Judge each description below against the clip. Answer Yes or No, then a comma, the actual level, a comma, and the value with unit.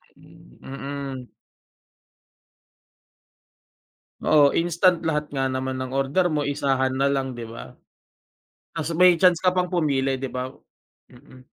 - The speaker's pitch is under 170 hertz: Yes, medium, 140 Hz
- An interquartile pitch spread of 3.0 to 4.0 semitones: Yes, average, 3.6 semitones